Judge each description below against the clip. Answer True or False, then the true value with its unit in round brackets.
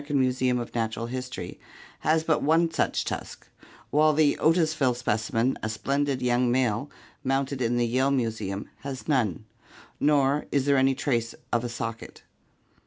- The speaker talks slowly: False (150 wpm)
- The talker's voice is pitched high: False (130 Hz)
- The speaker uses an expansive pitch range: False (3.3 semitones)